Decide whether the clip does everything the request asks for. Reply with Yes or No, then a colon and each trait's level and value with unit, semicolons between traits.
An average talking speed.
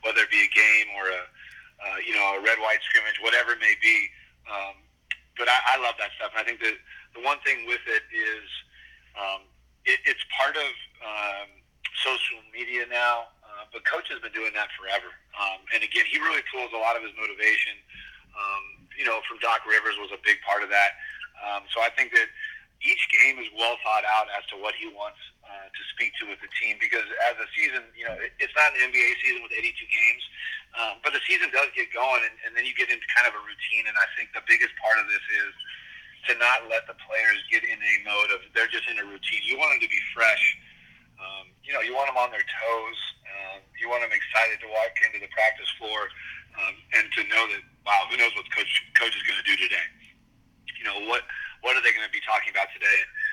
No: fast, 235 wpm